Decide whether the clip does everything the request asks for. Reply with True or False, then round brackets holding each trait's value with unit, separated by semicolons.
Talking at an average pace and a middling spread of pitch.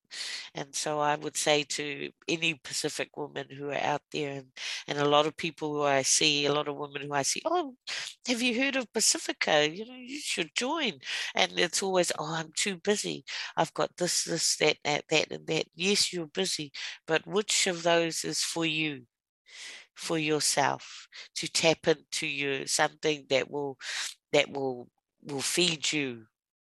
True (180 wpm; 3.8 semitones)